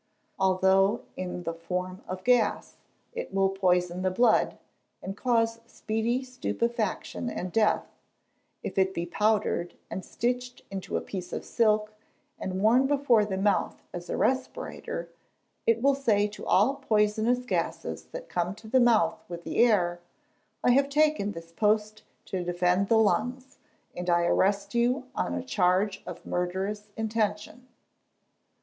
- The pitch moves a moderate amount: Yes, average, 4.4 semitones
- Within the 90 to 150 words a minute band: Yes, average, 145 wpm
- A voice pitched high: Yes, high, 210 Hz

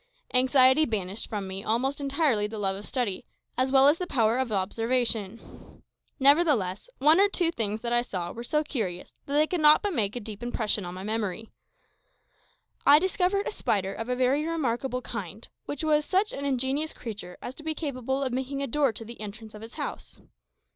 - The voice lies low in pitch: No, very high, 250 Hz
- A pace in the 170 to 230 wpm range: Yes, average, 200 wpm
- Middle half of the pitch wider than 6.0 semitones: No, average, 5.2 semitones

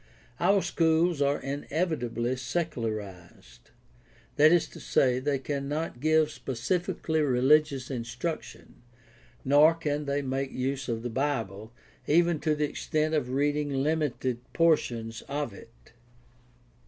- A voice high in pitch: No, medium, 140 Hz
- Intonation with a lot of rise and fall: No, average, 4.0 semitones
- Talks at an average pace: No, slow, 115 wpm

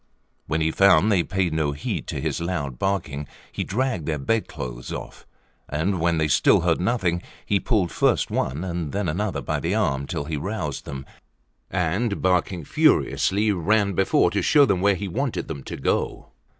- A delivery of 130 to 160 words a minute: No, average, 185 wpm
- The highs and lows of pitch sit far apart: No, average, 4.5 semitones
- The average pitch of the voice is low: Yes, very low, 90 Hz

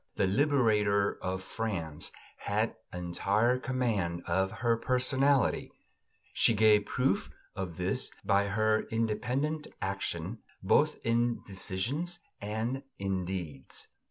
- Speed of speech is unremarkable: No, slow, 105 wpm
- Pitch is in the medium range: No, low, 105 Hz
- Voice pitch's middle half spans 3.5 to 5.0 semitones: Yes, average, 4.4 semitones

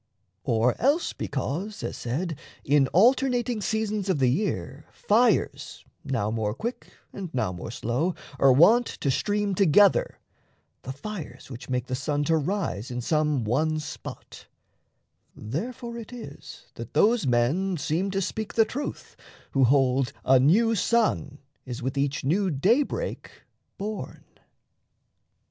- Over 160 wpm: No, slow, 135 wpm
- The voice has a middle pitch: Yes, medium, 160 Hz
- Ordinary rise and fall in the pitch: No, wide, 8.3 semitones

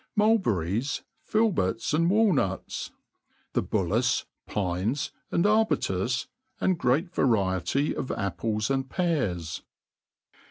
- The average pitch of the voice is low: Yes, low, 130 Hz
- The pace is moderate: No, slow, 95 wpm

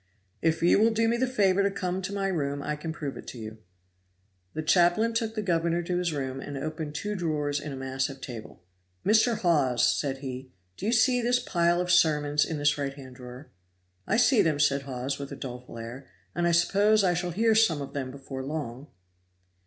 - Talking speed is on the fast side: Yes, fast, 215 wpm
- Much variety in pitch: Yes, wide, 6.0 semitones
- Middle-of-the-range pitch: Yes, medium, 155 Hz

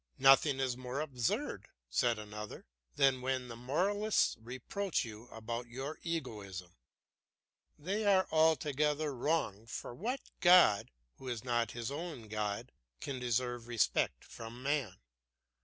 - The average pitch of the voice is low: Yes, low, 125 Hz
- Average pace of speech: No, slow, 125 wpm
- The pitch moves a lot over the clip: No, average, 4.8 semitones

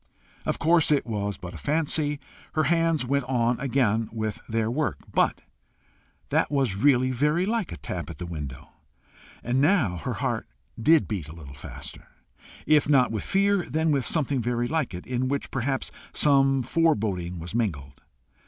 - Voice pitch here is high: No, low, 130 Hz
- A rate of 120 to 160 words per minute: No, average, 170 wpm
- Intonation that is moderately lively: No, wide, 5.9 semitones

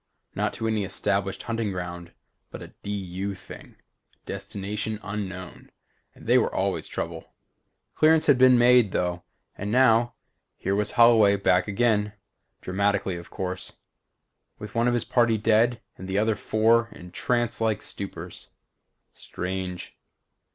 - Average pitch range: Yes, average, 3.4 semitones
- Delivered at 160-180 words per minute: No, average, 140 wpm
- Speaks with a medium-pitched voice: No, low, 105 Hz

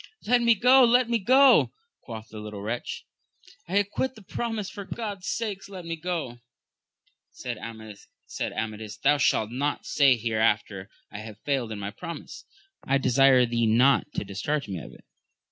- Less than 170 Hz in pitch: Yes, low, 135 Hz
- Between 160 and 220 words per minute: Yes, average, 170 wpm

